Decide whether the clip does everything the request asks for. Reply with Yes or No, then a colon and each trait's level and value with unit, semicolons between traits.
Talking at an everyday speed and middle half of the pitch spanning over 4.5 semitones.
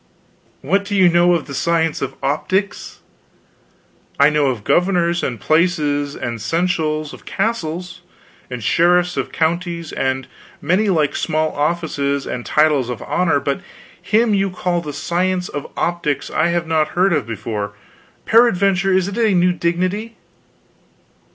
No: average, 145 wpm; average, 3.9 semitones